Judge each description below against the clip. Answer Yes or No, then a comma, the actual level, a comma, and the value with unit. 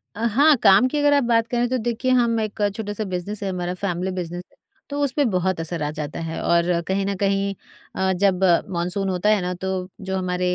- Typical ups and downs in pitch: Yes, average, 4.1 semitones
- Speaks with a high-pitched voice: Yes, high, 195 Hz